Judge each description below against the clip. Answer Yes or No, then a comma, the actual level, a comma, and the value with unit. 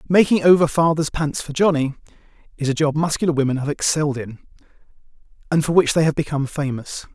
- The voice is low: No, medium, 150 Hz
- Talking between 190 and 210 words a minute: No, average, 175 wpm